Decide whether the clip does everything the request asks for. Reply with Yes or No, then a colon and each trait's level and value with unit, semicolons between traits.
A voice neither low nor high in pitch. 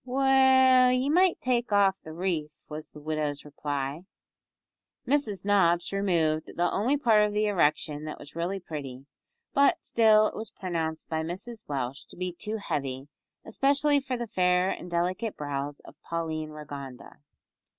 Yes: medium, 180 Hz